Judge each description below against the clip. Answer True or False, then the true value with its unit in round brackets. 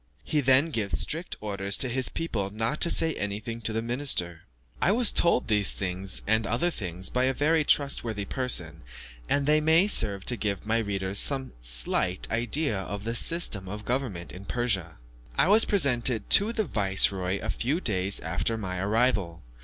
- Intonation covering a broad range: True (6.0 semitones)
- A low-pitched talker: True (110 Hz)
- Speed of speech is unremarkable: True (180 wpm)